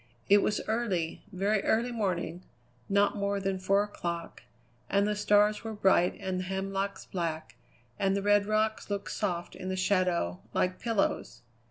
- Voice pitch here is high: Yes, high, 195 Hz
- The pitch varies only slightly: Yes, narrow, 2.0 semitones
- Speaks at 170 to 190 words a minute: No, average, 160 wpm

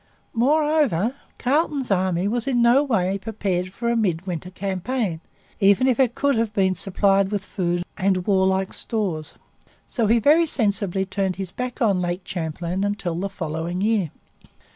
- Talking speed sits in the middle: Yes, average, 155 wpm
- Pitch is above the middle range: Yes, high, 195 Hz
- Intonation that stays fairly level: No, average, 4.4 semitones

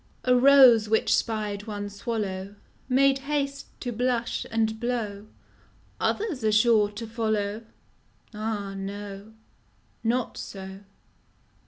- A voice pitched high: Yes, high, 220 Hz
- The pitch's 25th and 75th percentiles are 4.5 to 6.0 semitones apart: No, average, 3.2 semitones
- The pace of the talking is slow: Yes, slow, 120 wpm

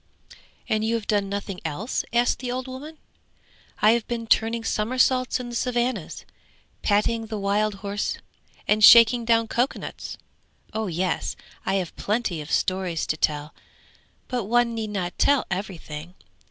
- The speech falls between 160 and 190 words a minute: No, average, 150 wpm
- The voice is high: Yes, high, 215 Hz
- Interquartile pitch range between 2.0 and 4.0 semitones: Yes, average, 3.6 semitones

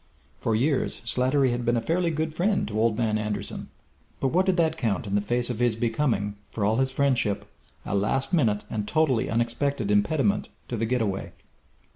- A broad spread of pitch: No, average, 4.7 semitones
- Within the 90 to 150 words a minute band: No, average, 195 wpm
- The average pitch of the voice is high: No, low, 120 Hz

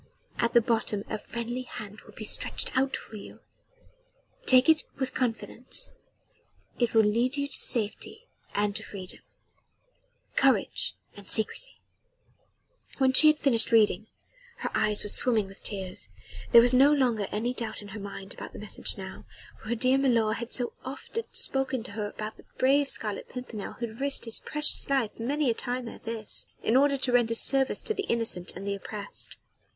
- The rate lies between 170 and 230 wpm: Yes, average, 180 wpm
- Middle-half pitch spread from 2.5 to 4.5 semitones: Yes, average, 3.7 semitones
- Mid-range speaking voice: No, high, 235 Hz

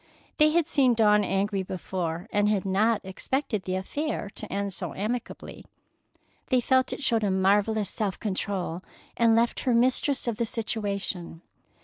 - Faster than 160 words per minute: No, average, 155 wpm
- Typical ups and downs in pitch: Yes, average, 3.7 semitones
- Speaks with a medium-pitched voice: No, high, 210 Hz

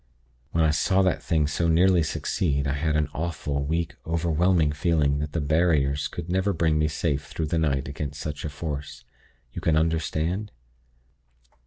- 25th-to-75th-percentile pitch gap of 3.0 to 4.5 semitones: No, narrow, 2.5 semitones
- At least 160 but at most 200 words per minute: Yes, average, 170 wpm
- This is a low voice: Yes, very low, 80 Hz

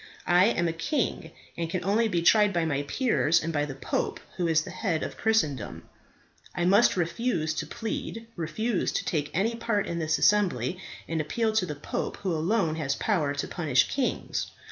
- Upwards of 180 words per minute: Yes, average, 190 wpm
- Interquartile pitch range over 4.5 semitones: Yes, average, 5.3 semitones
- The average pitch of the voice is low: No, medium, 170 Hz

